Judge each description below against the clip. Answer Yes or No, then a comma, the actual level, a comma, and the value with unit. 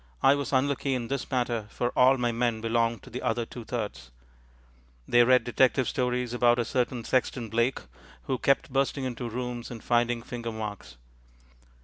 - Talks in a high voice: No, low, 120 Hz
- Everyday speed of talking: Yes, average, 170 wpm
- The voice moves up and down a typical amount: No, narrow, 1.7 semitones